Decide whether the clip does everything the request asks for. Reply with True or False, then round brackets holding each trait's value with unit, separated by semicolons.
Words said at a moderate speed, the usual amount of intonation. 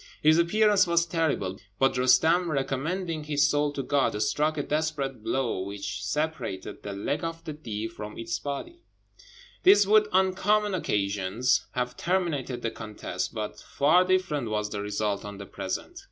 False (160 wpm; 7.9 semitones)